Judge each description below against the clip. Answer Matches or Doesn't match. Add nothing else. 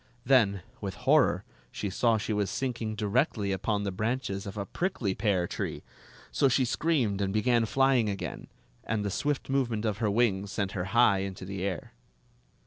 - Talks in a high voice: Doesn't match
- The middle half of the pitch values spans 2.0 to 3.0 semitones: Doesn't match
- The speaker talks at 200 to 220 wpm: Doesn't match